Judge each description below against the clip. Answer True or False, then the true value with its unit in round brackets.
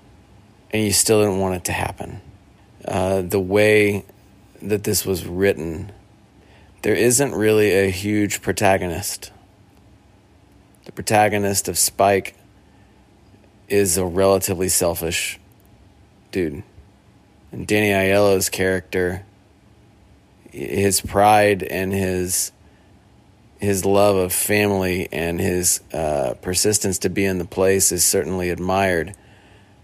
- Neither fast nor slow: False (110 wpm)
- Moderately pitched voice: False (100 Hz)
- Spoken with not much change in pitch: True (1.4 semitones)